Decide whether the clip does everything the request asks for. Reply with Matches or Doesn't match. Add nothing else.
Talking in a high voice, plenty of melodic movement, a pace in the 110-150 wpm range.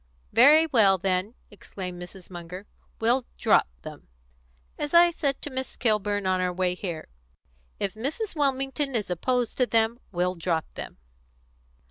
Matches